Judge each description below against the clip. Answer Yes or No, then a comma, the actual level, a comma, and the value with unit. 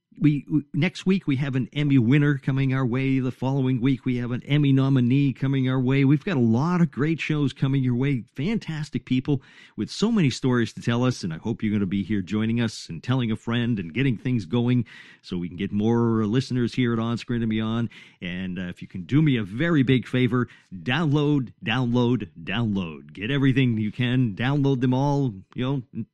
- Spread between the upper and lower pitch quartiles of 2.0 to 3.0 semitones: No, average, 3.5 semitones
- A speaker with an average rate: No, fast, 220 wpm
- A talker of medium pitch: No, low, 125 Hz